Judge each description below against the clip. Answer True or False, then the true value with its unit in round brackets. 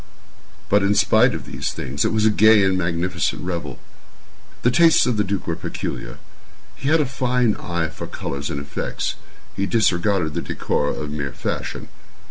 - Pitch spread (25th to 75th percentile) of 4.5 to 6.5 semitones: True (5.2 semitones)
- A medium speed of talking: True (175 wpm)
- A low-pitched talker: True (95 Hz)